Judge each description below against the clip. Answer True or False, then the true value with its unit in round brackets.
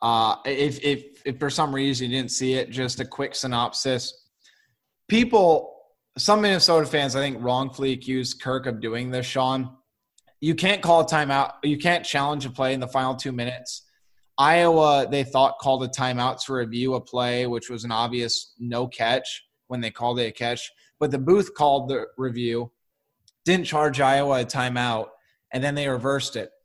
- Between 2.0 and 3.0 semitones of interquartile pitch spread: True (2.5 semitones)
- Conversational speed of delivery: True (180 wpm)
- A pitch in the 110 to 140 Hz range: True (130 Hz)